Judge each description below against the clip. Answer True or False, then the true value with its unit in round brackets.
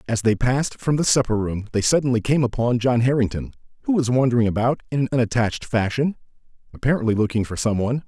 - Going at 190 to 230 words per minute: True (195 wpm)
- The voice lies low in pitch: True (120 Hz)